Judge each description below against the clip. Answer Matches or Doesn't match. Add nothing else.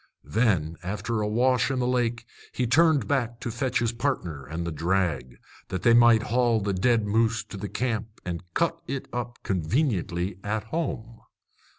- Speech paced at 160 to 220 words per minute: Matches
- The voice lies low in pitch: Matches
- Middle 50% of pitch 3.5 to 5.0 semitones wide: Matches